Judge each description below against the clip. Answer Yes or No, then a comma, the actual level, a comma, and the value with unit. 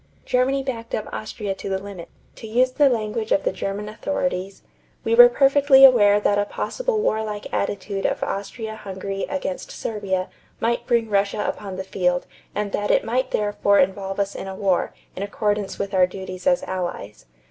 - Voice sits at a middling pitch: No, high, 205 Hz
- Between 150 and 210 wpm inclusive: Yes, average, 180 wpm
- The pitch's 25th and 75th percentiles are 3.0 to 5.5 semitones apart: Yes, average, 3.4 semitones